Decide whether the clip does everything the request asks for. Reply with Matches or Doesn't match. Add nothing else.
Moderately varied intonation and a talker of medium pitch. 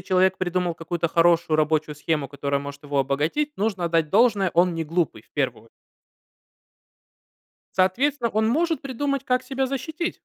Doesn't match